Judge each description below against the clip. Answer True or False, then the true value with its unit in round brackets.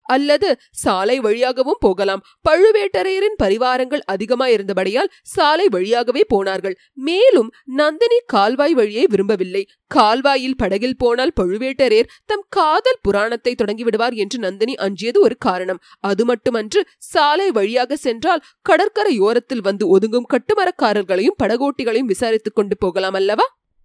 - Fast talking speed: False (105 wpm)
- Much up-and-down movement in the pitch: True (6.6 semitones)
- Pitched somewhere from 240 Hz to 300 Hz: True (245 Hz)